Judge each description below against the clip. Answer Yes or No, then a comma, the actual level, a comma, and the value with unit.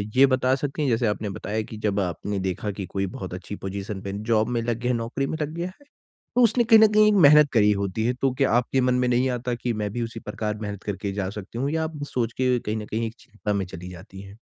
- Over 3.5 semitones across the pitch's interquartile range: Yes, average, 4.6 semitones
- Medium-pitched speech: No, low, 115 Hz